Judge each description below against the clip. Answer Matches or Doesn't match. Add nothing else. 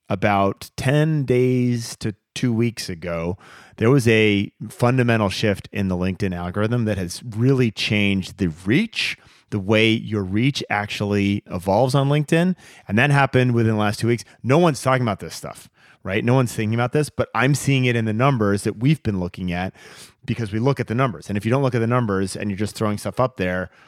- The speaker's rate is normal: Doesn't match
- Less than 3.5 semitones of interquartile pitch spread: Doesn't match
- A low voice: Matches